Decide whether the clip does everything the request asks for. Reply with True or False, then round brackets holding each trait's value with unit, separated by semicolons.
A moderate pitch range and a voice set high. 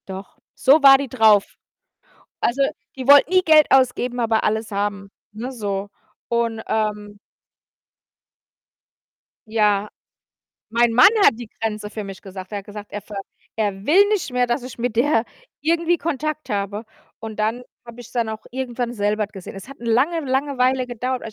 True (3.9 semitones; 235 Hz)